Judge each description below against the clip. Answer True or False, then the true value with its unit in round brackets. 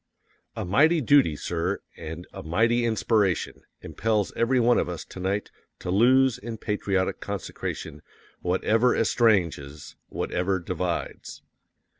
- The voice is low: True (100 Hz)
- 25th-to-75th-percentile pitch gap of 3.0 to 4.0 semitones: False (4.9 semitones)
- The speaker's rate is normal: False (120 wpm)